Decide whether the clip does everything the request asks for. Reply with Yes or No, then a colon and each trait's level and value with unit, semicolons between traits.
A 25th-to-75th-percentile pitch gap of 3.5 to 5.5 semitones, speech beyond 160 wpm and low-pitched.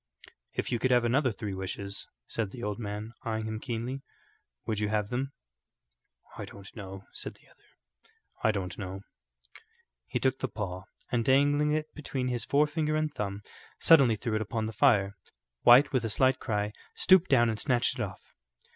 Yes: average, 4.3 semitones; average, 180 wpm; low, 115 Hz